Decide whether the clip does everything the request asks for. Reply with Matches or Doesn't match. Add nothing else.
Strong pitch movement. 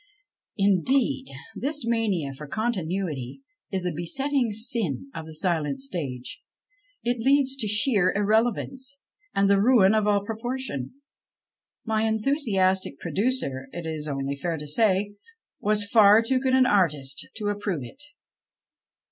Matches